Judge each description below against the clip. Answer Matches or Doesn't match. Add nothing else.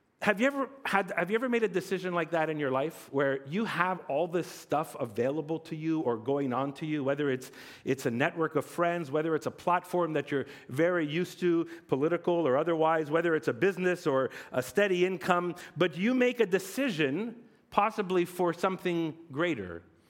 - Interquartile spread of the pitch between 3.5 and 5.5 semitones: Matches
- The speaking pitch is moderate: Matches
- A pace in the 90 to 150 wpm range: Doesn't match